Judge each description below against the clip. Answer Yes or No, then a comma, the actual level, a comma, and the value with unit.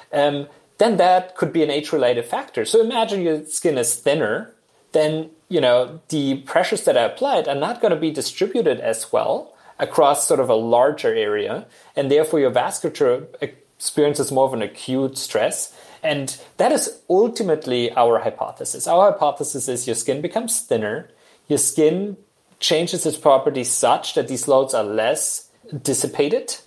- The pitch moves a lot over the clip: Yes, wide, 8.4 semitones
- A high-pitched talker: No, medium, 155 Hz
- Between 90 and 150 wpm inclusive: No, average, 160 wpm